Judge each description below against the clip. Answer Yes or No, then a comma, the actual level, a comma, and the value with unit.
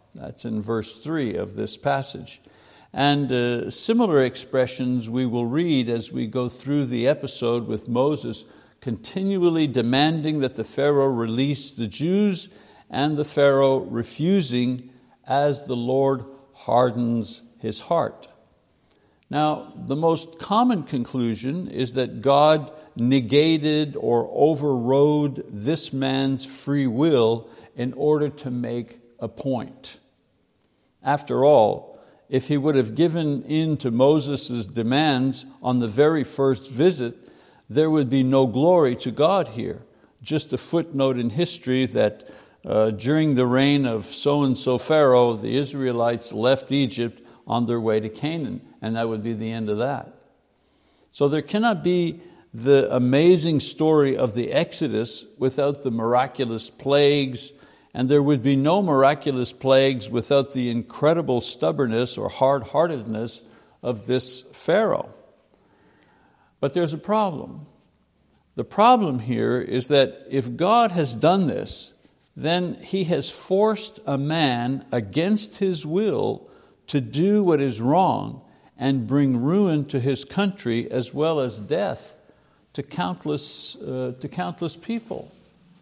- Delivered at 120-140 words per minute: Yes, slow, 135 wpm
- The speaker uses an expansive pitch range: No, average, 3.8 semitones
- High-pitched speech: No, low, 135 Hz